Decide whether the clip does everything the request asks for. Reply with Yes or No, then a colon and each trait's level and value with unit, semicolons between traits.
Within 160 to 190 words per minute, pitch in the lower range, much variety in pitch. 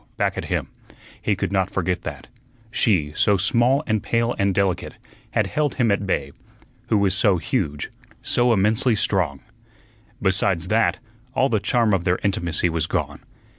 No: average, 165 wpm; low, 100 Hz; average, 3.7 semitones